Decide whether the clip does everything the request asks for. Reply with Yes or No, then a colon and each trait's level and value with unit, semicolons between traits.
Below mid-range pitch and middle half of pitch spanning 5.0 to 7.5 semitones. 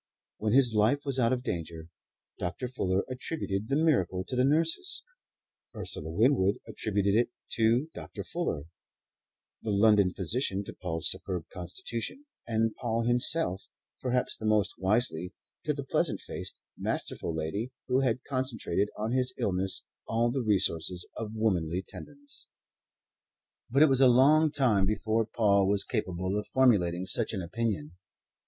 Yes: low, 110 Hz; average, 5.3 semitones